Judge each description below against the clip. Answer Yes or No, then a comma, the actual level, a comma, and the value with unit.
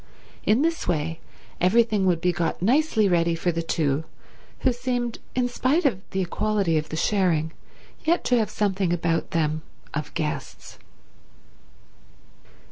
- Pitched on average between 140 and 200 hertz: Yes, medium, 185 Hz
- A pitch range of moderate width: No, wide, 6.2 semitones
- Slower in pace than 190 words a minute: Yes, average, 140 wpm